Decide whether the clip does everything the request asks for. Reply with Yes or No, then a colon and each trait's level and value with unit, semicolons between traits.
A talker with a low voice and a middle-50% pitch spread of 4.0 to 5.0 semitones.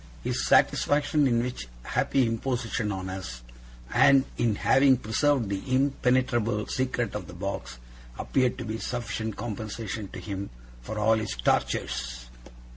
Yes: low, 110 Hz; average, 4.6 semitones